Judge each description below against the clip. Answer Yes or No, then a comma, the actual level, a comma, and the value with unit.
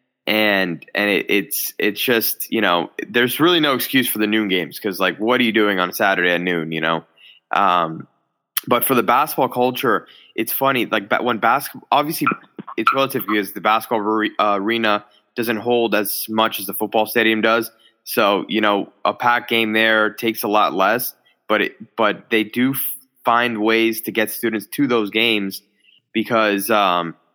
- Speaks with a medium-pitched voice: No, low, 110 Hz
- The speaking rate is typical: Yes, average, 185 wpm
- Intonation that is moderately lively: No, narrow, 2.2 semitones